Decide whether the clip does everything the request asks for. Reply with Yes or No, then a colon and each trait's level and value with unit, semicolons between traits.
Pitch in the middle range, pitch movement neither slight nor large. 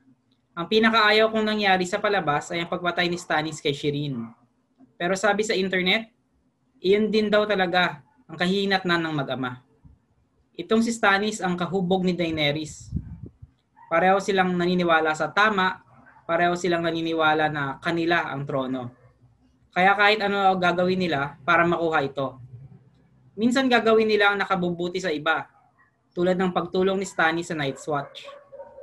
Yes: medium, 175 Hz; average, 4.8 semitones